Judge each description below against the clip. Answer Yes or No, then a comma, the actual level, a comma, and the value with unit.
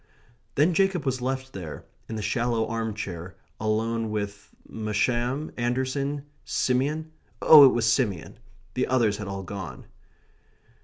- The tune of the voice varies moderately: Yes, average, 3.9 semitones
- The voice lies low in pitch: Yes, low, 120 Hz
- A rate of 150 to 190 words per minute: No, slow, 135 wpm